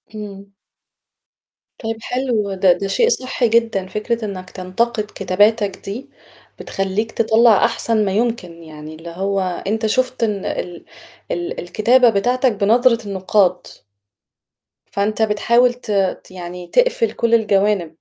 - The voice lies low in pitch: No, high, 210 Hz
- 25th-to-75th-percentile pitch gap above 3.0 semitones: Yes, average, 3.5 semitones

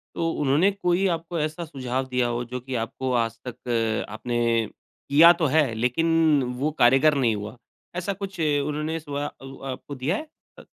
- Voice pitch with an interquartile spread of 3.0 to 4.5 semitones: No, average, 4.9 semitones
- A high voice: No, medium, 140 Hz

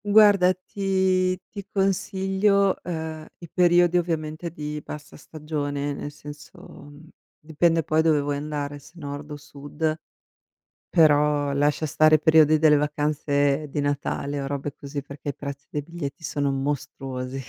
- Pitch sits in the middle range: Yes, medium, 150 Hz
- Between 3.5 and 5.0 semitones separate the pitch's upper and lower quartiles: No, average, 2.8 semitones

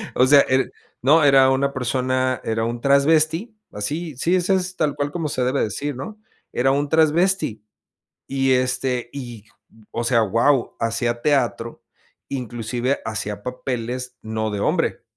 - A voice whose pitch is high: No, low, 130 Hz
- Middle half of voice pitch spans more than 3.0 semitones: Yes, average, 3.5 semitones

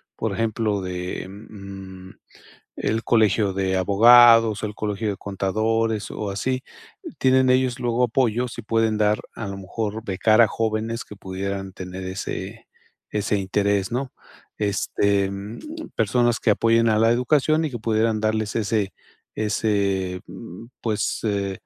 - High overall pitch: No, low, 110 Hz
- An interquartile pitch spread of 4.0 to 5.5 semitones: No, narrow, 2.6 semitones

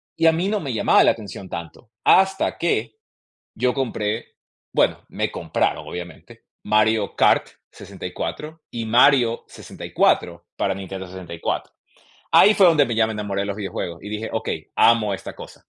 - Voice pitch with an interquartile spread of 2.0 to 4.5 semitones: No, wide, 5.4 semitones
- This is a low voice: Yes, low, 110 Hz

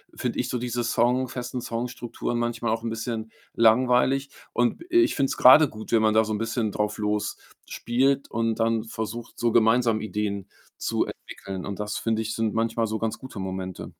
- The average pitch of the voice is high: No, low, 115 Hz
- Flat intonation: Yes, narrow, 2.0 semitones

